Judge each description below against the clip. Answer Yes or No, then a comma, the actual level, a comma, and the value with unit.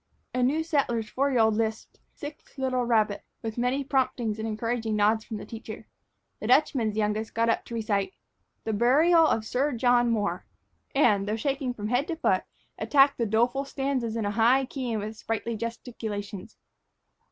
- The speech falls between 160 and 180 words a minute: Yes, average, 175 wpm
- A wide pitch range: No, average, 3.3 semitones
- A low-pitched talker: No, high, 230 Hz